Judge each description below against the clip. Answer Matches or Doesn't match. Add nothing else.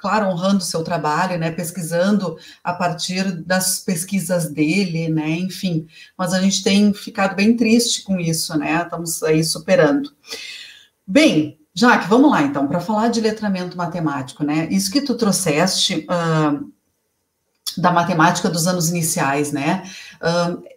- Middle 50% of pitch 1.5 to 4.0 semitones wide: Matches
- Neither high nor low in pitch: Matches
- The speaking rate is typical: Matches